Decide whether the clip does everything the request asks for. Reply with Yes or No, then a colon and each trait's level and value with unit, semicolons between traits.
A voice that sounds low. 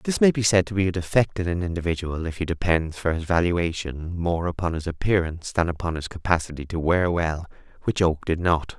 Yes: very low, 85 Hz